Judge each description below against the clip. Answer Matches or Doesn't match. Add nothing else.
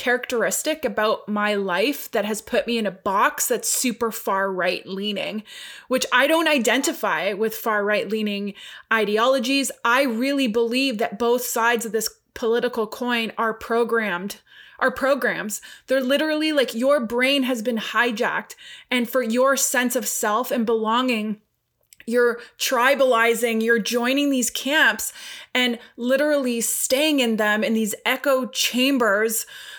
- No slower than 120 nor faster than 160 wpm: Matches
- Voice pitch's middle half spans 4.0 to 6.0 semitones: Doesn't match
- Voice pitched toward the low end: Doesn't match